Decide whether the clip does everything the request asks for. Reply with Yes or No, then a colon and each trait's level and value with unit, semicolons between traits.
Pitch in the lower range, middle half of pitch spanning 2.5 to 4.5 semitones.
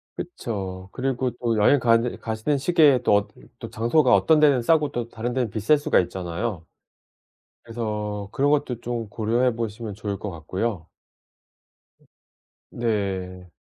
Yes: low, 115 Hz; average, 3.7 semitones